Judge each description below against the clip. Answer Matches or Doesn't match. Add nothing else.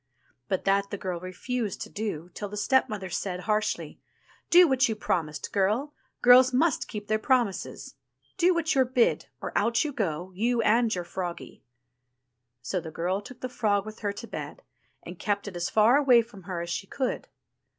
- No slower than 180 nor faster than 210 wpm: Matches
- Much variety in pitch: Doesn't match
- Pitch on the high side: Matches